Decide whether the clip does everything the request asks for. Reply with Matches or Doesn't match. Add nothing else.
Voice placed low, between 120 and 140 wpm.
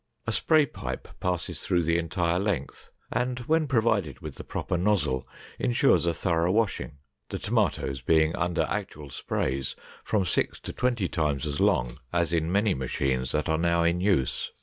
Doesn't match